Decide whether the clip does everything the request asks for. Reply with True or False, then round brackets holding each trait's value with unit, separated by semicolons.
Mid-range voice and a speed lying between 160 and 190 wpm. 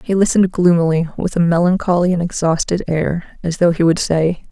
True (175 Hz; 185 wpm)